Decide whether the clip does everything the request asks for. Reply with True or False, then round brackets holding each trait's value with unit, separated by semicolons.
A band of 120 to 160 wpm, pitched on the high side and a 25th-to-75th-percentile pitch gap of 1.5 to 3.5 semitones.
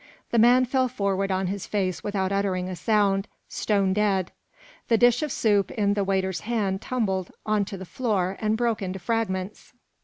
False (175 wpm; 200 Hz; 2.8 semitones)